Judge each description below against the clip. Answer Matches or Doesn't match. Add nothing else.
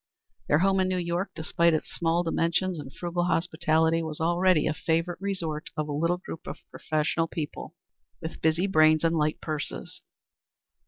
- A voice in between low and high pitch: Matches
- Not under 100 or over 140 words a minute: Doesn't match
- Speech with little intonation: Matches